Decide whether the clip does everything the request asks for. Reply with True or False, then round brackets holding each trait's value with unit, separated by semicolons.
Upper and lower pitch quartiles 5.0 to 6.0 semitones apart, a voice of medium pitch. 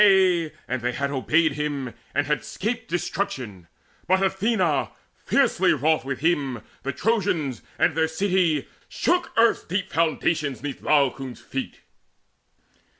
True (5.4 semitones; 155 Hz)